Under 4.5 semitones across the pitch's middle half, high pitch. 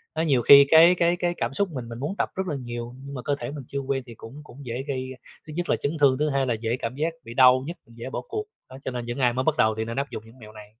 No: average, 3.8 semitones; low, 130 Hz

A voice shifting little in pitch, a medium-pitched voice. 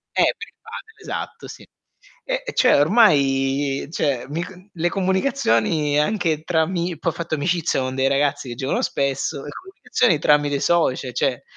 No: average, 4.8 semitones; medium, 150 Hz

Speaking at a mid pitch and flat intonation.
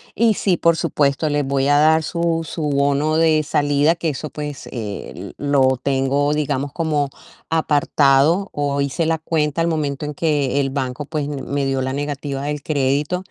Yes: medium, 145 Hz; narrow, 2.3 semitones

